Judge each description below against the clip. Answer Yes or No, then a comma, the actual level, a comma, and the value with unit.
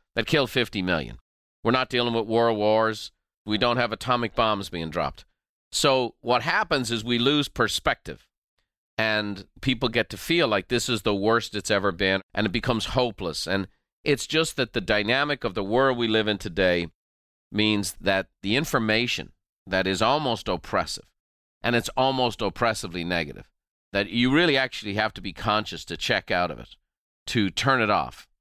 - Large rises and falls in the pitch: No, average, 3.8 semitones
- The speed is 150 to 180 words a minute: Yes, average, 175 wpm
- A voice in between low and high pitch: No, low, 110 Hz